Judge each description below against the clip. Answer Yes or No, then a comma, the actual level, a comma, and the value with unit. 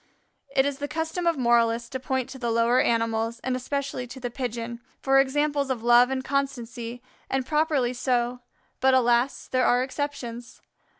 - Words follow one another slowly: No, average, 170 wpm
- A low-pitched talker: No, very high, 255 Hz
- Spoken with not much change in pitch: Yes, narrow, 2.3 semitones